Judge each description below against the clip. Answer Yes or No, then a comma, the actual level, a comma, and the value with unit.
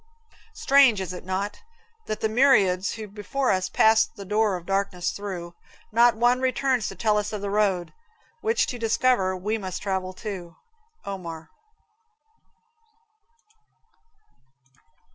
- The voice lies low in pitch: No, high, 205 Hz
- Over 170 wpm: No, slow, 135 wpm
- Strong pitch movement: No, average, 3.4 semitones